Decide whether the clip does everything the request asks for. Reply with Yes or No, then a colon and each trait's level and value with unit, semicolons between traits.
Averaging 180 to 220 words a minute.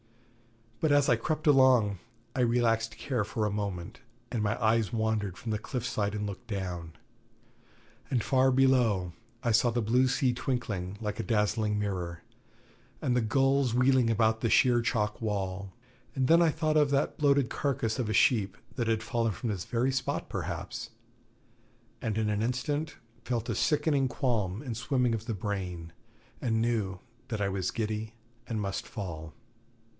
No: average, 170 wpm